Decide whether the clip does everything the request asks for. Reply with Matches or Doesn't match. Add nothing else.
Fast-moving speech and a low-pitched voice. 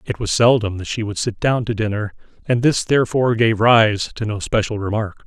Matches